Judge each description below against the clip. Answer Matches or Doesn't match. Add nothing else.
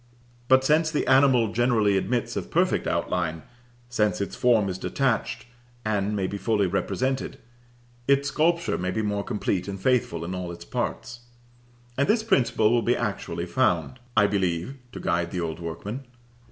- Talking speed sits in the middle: Matches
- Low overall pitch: Matches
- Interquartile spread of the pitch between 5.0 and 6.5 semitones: Matches